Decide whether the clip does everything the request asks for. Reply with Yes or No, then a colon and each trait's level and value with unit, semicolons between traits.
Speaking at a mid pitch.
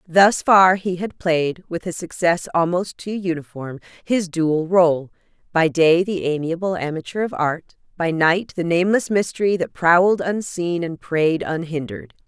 Yes: medium, 170 Hz